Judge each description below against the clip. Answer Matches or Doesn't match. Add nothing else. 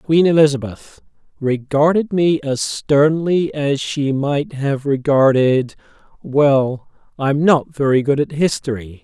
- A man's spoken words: Matches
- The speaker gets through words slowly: Matches